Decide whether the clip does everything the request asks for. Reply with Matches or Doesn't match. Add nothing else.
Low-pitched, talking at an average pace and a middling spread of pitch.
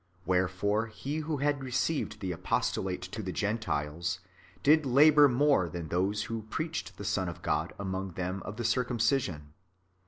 Doesn't match